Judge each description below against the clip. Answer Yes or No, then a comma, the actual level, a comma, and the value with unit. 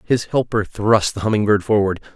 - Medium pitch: No, low, 105 Hz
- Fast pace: No, average, 195 wpm